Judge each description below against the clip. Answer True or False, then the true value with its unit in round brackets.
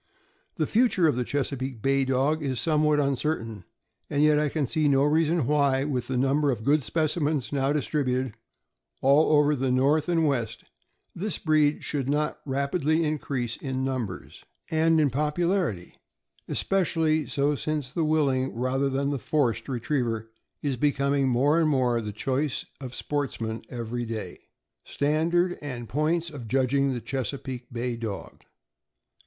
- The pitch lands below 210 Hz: True (140 Hz)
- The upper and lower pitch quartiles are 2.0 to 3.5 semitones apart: True (3.1 semitones)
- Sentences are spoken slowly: False (150 wpm)